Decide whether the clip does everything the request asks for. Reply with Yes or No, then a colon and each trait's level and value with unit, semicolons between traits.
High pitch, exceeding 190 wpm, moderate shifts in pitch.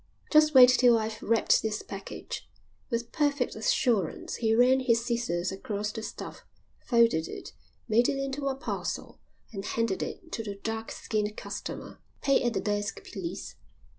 No: high, 230 Hz; average, 160 wpm; average, 3.3 semitones